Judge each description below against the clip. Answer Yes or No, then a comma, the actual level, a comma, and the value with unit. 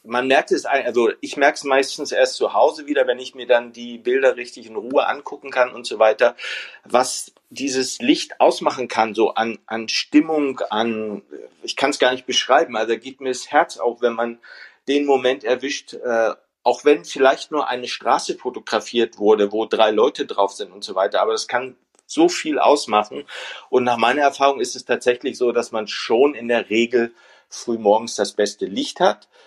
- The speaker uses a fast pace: Yes, fast, 200 wpm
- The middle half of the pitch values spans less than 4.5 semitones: No, wide, 5.5 semitones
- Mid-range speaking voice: No, low, 130 Hz